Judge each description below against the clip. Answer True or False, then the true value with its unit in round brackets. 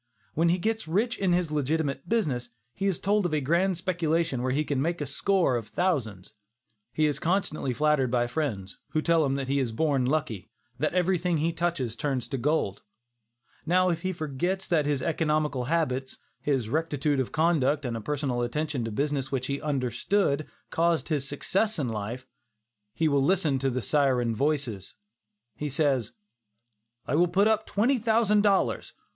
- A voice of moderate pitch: True (150 Hz)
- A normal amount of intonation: True (4.7 semitones)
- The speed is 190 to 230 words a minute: False (180 wpm)